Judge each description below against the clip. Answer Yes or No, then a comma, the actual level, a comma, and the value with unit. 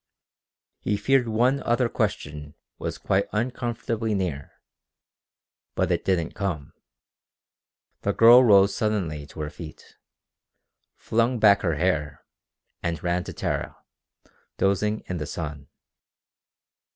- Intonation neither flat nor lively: No, wide, 6.0 semitones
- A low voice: Yes, low, 100 Hz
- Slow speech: Yes, slow, 115 wpm